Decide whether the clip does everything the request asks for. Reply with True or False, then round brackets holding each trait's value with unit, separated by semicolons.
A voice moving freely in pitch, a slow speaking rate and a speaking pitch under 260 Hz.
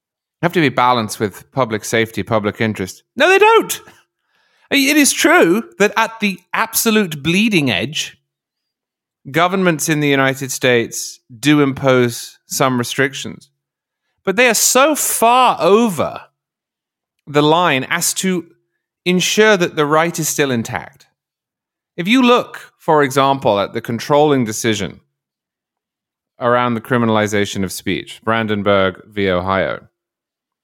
True (8.1 semitones; 125 wpm; 140 Hz)